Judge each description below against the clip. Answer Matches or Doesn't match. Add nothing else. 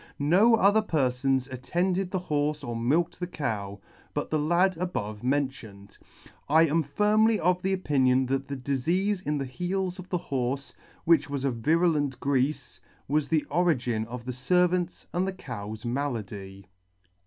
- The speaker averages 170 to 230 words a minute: Doesn't match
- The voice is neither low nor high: Matches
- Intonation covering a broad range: Matches